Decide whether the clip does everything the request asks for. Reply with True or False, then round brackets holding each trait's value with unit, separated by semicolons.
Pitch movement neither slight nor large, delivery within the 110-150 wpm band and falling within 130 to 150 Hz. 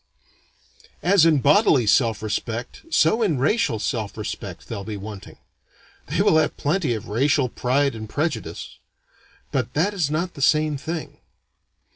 False (5.8 semitones; 145 wpm; 140 Hz)